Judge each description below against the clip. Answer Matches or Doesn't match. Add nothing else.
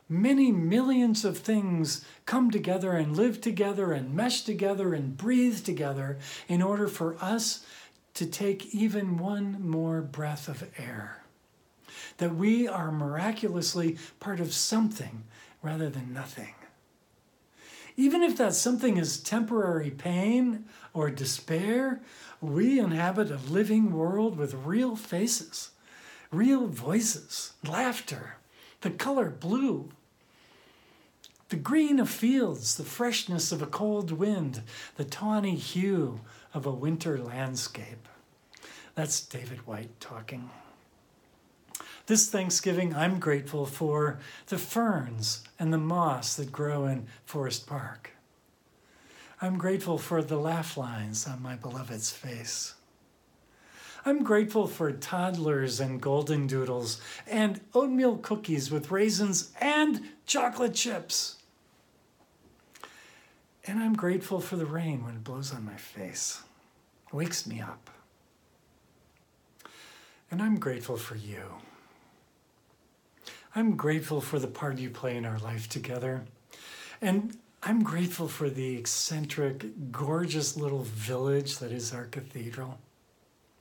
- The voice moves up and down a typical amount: Doesn't match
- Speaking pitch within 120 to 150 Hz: Doesn't match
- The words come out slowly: Matches